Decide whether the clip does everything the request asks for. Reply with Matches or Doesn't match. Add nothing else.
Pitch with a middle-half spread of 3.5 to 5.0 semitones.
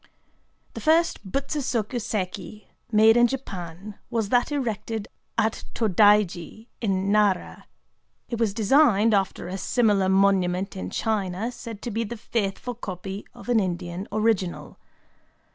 Doesn't match